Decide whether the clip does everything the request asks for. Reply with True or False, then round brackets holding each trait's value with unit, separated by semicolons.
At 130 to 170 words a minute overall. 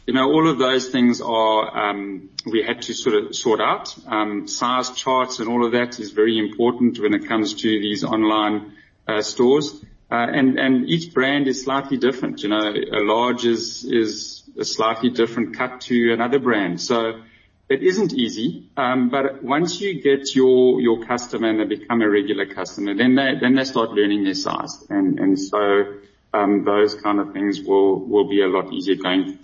False (195 wpm)